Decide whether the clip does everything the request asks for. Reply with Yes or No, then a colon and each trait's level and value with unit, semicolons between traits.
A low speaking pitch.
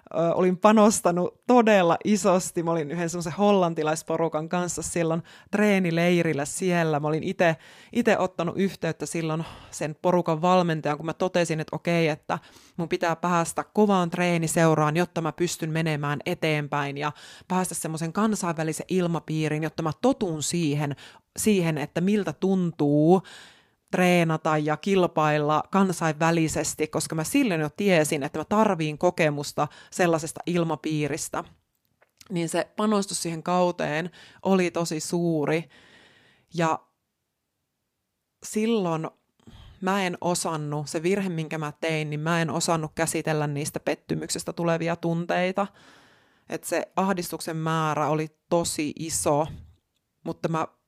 No: medium, 165 Hz